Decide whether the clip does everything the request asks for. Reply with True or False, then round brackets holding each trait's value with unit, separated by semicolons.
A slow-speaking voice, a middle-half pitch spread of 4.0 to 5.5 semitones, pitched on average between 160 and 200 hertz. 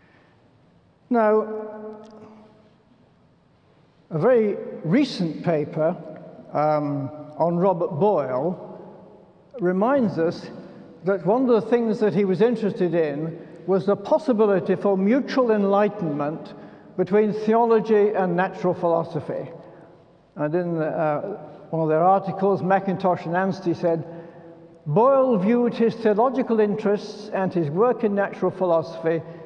True (110 wpm; 4.4 semitones; 190 Hz)